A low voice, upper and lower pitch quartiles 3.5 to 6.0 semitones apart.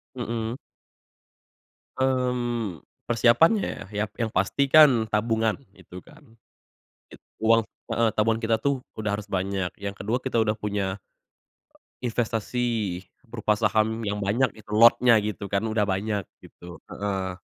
No: low, 110 Hz; average, 2.7 semitones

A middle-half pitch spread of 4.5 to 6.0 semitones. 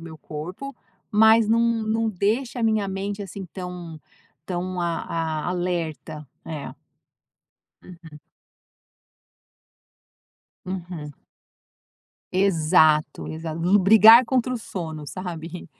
Yes: average, 5.0 semitones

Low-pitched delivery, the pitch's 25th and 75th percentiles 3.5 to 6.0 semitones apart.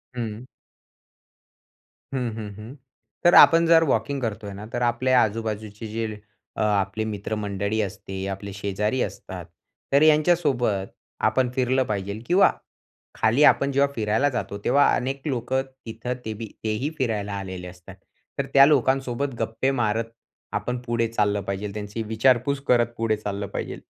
Yes: low, 115 Hz; average, 4.1 semitones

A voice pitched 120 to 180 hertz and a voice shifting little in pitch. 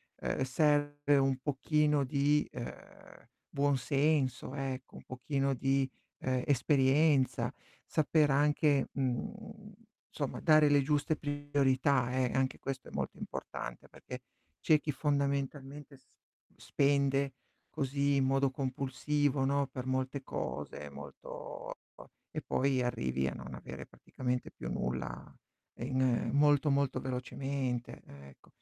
Yes: low, 135 Hz; narrow, 1.9 semitones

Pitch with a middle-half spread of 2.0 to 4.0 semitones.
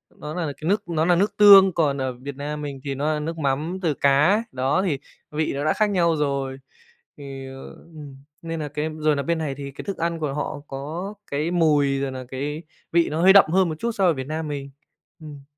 Yes: average, 3.4 semitones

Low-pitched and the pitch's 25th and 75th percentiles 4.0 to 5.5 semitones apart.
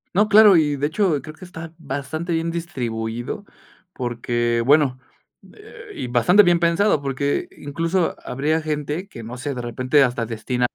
No: medium, 145 Hz; average, 5.2 semitones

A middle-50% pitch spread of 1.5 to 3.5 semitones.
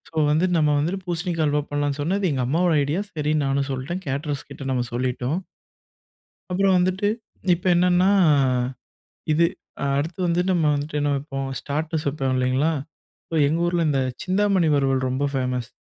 No: average, 4.4 semitones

